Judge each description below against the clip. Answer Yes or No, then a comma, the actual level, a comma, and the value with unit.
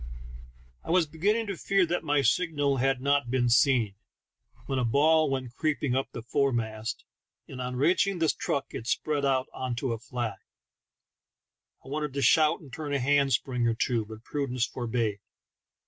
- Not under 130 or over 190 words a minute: Yes, average, 175 wpm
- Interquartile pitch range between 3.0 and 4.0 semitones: Yes, average, 3.6 semitones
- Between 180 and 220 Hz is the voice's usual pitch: No, low, 135 Hz